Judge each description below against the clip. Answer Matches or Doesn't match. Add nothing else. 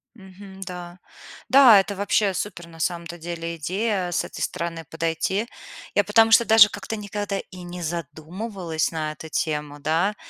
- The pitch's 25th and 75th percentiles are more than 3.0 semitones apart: Matches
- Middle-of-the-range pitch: Matches